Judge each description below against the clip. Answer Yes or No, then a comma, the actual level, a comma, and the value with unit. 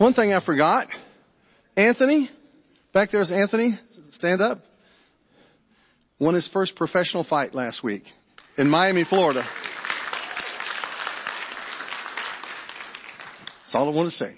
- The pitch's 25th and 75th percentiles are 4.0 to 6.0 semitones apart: Yes, wide, 5.5 semitones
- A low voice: No, high, 190 Hz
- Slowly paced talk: Yes, slow, 115 wpm